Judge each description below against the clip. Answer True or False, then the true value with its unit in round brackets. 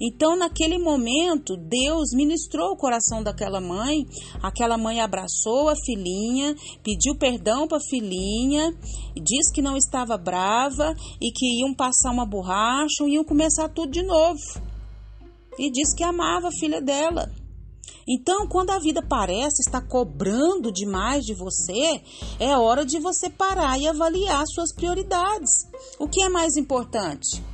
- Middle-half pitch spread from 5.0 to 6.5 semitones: True (5.6 semitones)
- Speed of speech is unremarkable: True (150 wpm)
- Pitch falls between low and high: False (285 Hz)